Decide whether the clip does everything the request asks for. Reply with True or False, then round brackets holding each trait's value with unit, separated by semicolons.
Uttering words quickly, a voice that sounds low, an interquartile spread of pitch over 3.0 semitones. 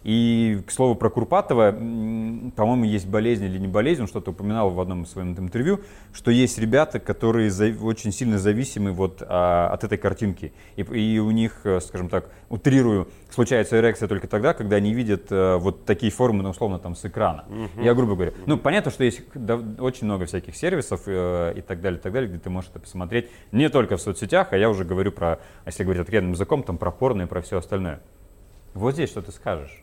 True (195 wpm; 105 Hz; 3.7 semitones)